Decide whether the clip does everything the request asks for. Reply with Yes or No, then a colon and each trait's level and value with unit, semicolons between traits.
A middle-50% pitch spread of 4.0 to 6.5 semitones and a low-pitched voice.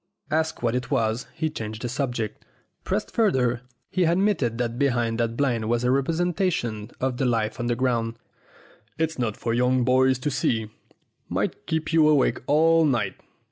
Yes: average, 4.6 semitones; low, 125 Hz